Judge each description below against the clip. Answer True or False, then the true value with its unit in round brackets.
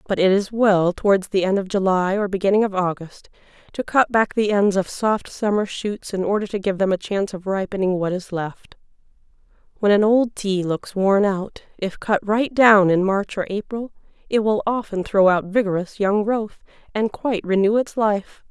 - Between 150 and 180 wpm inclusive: False (200 wpm)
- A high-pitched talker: True (200 Hz)